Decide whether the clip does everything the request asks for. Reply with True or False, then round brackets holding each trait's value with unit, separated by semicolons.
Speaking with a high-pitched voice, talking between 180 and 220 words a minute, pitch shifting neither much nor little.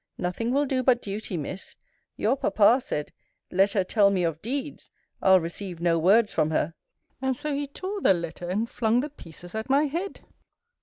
False (210 Hz; 190 wpm; 6.9 semitones)